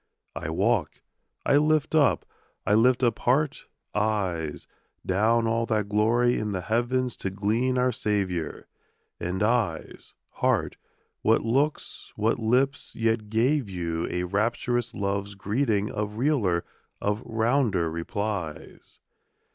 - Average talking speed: No, slow, 125 wpm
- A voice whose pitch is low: Yes, low, 110 Hz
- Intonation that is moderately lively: Yes, average, 3.7 semitones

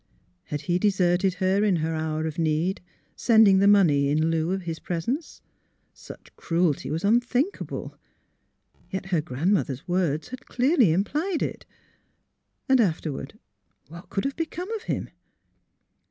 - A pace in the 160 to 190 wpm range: No, average, 150 wpm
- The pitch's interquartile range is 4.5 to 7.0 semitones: Yes, wide, 5.6 semitones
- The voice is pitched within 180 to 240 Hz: Yes, medium, 185 Hz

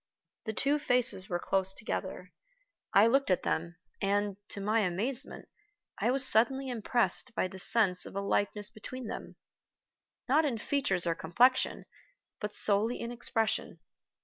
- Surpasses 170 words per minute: No, average, 150 wpm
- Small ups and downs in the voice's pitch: No, average, 4.3 semitones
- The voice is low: No, high, 215 Hz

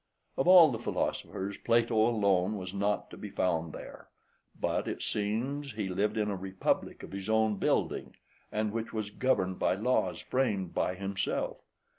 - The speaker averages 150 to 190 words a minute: Yes, average, 170 wpm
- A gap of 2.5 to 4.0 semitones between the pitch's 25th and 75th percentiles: Yes, average, 3.0 semitones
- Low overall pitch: Yes, low, 105 Hz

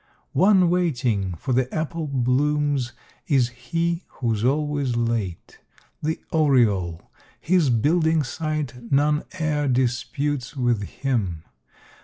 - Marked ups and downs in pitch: No, average, 4.1 semitones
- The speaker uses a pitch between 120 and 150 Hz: Yes, low, 135 Hz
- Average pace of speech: No, slow, 105 wpm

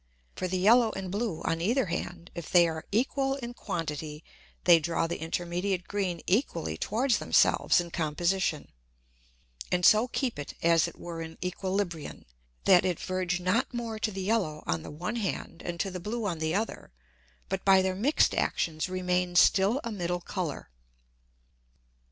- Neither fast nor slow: Yes, average, 170 wpm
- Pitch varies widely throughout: No, average, 3.5 semitones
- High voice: No, medium, 180 Hz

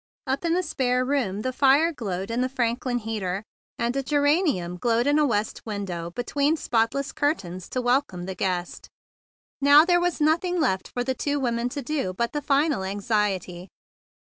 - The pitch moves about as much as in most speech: No, wide, 6.2 semitones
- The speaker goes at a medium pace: Yes, average, 190 wpm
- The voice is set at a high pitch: Yes, high, 245 Hz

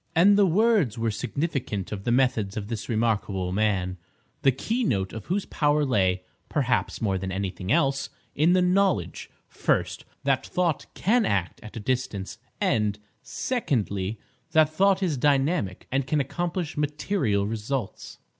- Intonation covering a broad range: Yes, wide, 8.3 semitones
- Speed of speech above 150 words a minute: No, average, 145 wpm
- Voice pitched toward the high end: No, low, 130 Hz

